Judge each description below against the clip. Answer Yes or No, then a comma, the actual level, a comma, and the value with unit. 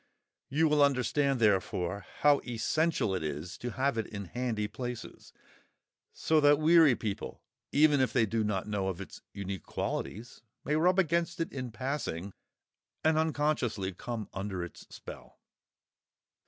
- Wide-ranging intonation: Yes, wide, 6.7 semitones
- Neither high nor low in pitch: No, low, 120 Hz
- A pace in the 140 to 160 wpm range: Yes, average, 145 wpm